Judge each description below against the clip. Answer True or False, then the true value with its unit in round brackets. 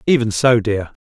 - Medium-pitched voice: False (110 Hz)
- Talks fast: False (175 wpm)